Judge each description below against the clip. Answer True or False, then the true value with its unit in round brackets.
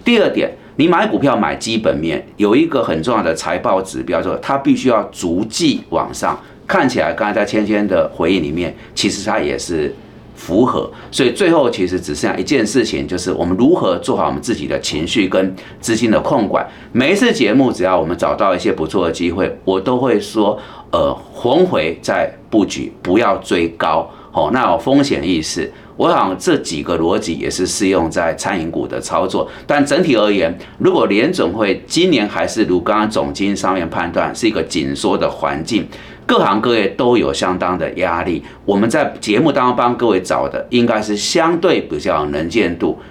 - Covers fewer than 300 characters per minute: True (285 characters per minute)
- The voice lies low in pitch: True (105 Hz)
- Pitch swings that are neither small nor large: True (4.5 semitones)